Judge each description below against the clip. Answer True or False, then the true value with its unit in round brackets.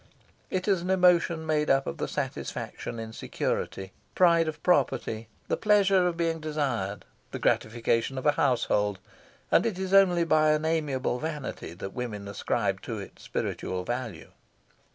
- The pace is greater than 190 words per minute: False (155 wpm)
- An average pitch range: False (6.8 semitones)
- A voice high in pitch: False (150 Hz)